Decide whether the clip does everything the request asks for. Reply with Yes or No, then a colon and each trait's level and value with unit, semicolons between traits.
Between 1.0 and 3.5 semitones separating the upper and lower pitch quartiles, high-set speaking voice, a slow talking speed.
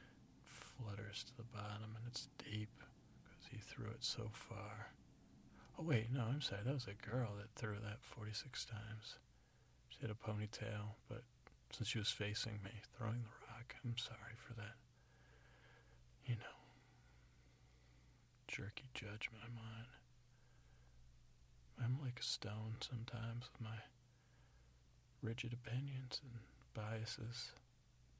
No: narrow, 2.6 semitones; low, 115 Hz; slow, 130 wpm